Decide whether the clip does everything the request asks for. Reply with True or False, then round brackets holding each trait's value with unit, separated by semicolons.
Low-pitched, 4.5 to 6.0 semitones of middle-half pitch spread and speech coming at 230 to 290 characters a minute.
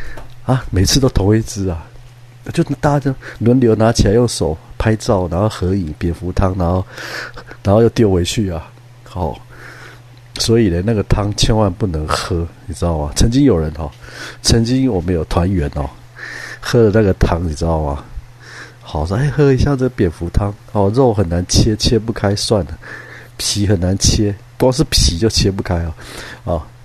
True (110 Hz; 5.2 semitones; 245 characters per minute)